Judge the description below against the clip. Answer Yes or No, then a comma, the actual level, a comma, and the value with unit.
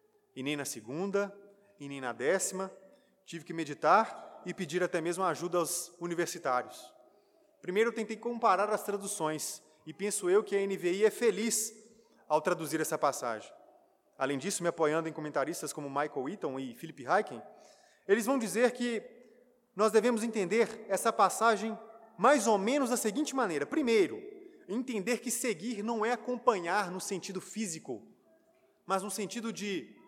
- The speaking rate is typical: Yes, average, 155 wpm